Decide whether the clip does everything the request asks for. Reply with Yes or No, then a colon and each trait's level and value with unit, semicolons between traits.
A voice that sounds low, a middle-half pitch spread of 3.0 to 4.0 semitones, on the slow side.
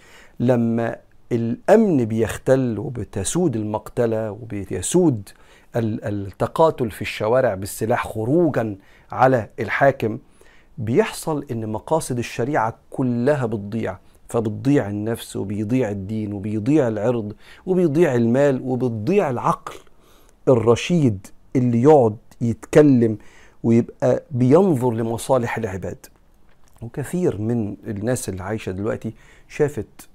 No: low, 115 Hz; average, 3.6 semitones; average, 90 wpm